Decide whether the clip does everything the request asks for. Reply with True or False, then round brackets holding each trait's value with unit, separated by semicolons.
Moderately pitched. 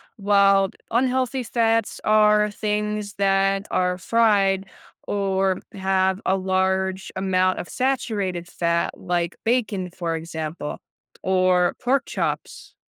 False (195 Hz)